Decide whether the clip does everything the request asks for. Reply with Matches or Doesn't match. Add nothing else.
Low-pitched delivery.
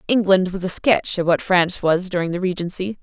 Doesn't match